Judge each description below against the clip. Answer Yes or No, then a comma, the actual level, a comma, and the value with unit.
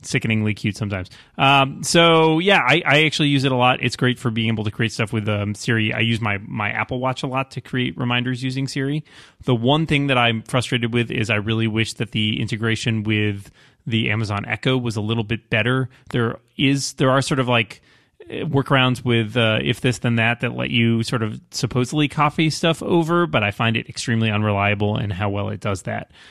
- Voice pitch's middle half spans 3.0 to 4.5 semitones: Yes, average, 3.4 semitones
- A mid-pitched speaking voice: No, low, 120 Hz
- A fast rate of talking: Yes, fast, 215 wpm